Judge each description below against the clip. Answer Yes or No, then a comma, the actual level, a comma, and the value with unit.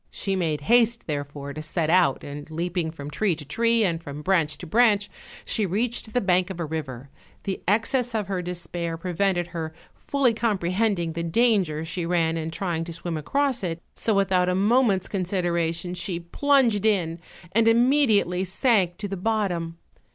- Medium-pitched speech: Yes, medium, 180 Hz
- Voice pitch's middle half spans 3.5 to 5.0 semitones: Yes, average, 4.5 semitones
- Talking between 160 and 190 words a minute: Yes, average, 175 wpm